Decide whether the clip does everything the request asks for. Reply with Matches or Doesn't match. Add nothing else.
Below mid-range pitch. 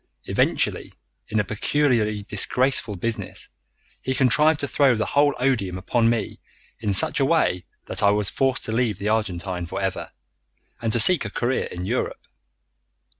Matches